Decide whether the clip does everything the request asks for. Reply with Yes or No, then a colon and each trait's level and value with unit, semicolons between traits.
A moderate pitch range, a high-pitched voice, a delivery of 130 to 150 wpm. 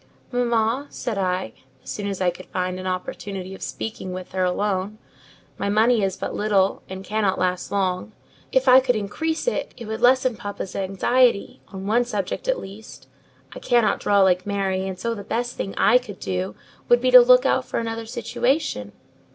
No: average, 4.3 semitones; high, 205 Hz; average, 190 wpm